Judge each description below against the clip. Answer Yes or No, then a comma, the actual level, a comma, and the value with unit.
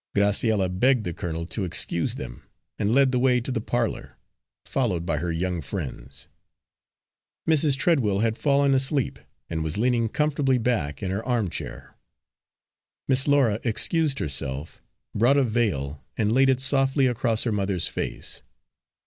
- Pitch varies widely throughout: Yes, wide, 6.7 semitones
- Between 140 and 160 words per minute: Yes, average, 150 wpm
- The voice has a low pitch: Yes, low, 115 Hz